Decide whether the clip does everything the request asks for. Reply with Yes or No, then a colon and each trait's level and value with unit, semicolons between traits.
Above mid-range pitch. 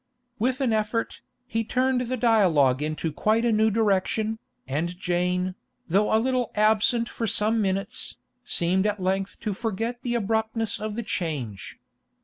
Yes: high, 215 Hz